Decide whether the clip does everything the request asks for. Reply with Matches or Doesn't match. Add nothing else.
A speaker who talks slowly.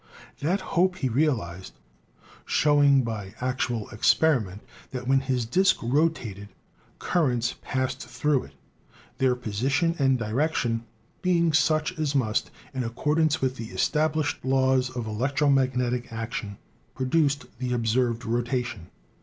Matches